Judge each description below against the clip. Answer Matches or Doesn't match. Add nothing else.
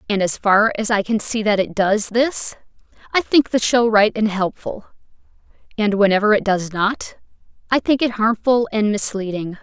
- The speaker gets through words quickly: Doesn't match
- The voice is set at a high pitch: Matches